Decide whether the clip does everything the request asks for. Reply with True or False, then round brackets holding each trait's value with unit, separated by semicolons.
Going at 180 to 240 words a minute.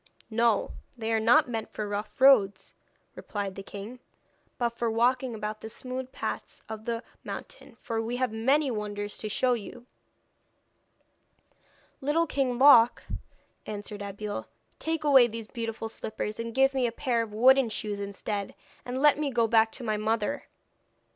False (160 wpm)